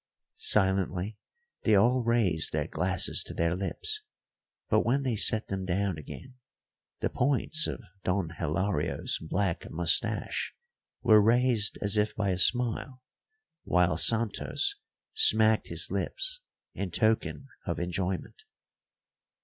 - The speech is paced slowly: Yes, slow, 120 wpm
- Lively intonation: No, average, 4.8 semitones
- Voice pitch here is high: No, low, 100 Hz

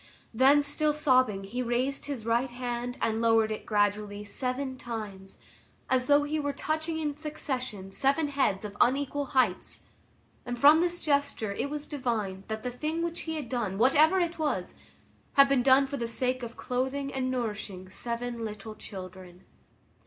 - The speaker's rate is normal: Yes, average, 165 wpm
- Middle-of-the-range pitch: No, very high, 255 Hz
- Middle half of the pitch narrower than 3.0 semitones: No, average, 4.7 semitones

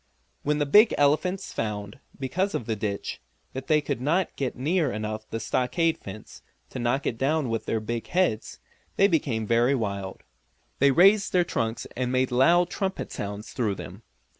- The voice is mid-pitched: No, low, 130 Hz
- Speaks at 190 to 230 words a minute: No, average, 175 wpm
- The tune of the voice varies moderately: No, wide, 6.5 semitones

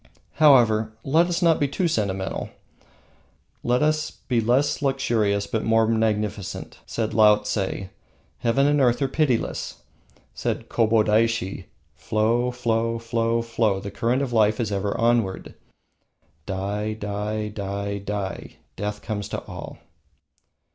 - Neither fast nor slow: No, slow, 125 wpm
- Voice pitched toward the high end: No, low, 110 Hz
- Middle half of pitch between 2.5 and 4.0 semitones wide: Yes, average, 2.8 semitones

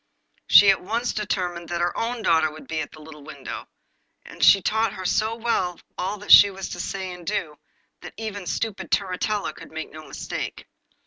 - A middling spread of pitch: Yes, average, 4.3 semitones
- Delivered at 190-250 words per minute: Yes, average, 195 wpm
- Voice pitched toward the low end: No, medium, 185 Hz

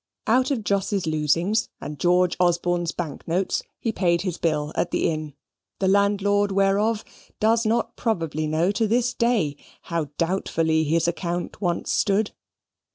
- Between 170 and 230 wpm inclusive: No, average, 150 wpm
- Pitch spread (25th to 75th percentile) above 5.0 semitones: No, average, 3.9 semitones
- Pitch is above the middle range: No, medium, 180 Hz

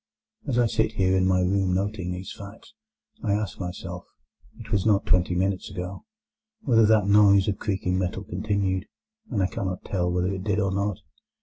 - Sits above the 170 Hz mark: No, very low, 95 Hz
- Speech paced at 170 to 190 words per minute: Yes, average, 185 wpm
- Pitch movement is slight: Yes, narrow, 1.9 semitones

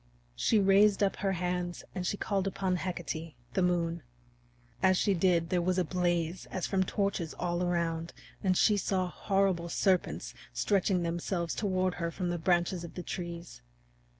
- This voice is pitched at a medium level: Yes, medium, 180 Hz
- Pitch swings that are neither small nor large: No, narrow, 1.9 semitones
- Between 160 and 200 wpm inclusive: Yes, average, 165 wpm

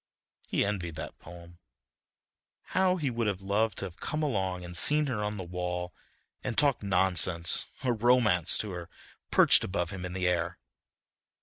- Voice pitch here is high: No, very low, 95 Hz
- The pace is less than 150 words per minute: No, average, 170 wpm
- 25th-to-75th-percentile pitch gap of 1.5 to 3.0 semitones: No, average, 4.2 semitones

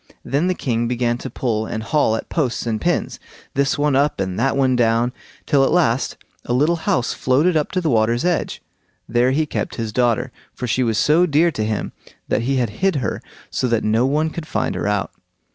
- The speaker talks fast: Yes, fast, 215 wpm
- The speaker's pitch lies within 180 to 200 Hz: No, low, 125 Hz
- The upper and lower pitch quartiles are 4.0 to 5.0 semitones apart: Yes, average, 4.4 semitones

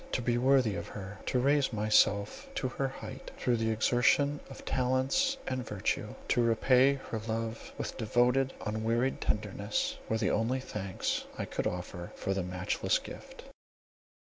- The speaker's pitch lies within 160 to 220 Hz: No, low, 115 Hz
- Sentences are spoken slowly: No, average, 155 wpm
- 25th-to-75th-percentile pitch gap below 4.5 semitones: Yes, average, 3.6 semitones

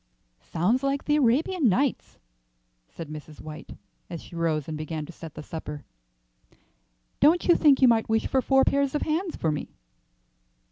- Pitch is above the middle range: Yes, high, 225 Hz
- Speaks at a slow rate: No, average, 170 wpm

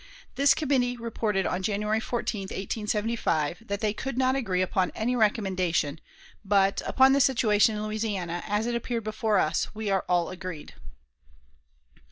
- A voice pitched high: Yes, high, 210 Hz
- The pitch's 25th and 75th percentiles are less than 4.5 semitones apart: Yes, average, 3.5 semitones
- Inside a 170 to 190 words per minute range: No, average, 150 wpm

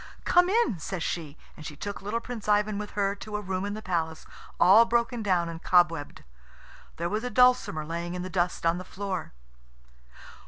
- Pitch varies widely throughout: No, average, 3.9 semitones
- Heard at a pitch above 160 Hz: Yes, high, 190 Hz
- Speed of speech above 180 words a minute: Yes, average, 195 wpm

